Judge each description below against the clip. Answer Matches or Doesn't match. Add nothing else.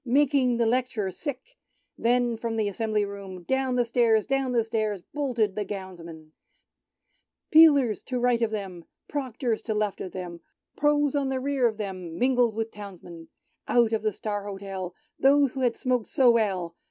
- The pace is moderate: Matches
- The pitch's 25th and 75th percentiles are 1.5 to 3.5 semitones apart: Doesn't match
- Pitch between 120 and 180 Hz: Doesn't match